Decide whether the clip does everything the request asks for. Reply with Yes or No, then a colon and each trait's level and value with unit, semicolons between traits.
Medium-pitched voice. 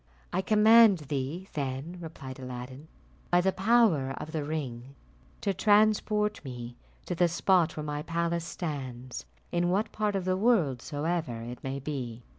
Yes: medium, 160 Hz